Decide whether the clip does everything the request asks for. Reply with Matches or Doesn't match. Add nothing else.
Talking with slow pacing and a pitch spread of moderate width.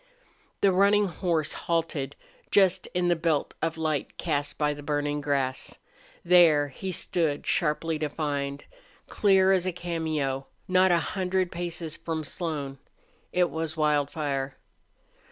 Matches